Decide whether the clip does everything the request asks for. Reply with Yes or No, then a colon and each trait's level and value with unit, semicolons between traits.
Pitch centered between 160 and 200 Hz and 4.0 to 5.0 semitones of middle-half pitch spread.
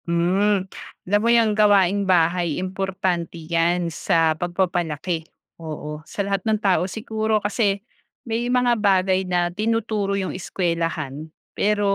No: high, 190 Hz; average, 3.3 semitones